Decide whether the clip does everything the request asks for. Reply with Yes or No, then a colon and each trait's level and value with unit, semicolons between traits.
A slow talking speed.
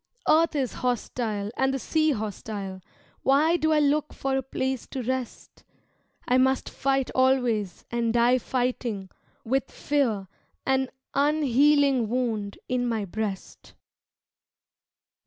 Yes: slow, 120 wpm